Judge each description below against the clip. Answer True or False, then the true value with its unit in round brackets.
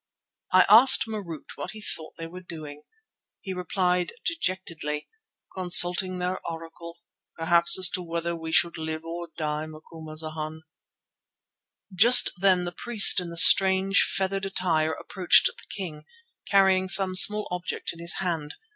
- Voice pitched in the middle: True (175 Hz)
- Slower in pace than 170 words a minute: True (140 wpm)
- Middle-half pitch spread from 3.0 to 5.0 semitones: False (2.6 semitones)